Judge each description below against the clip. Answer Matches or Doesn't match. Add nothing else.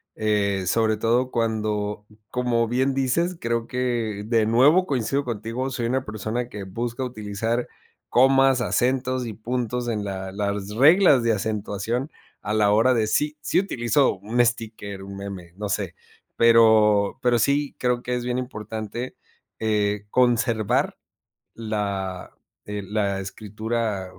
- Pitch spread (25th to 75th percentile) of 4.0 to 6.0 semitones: Doesn't match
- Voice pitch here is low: Matches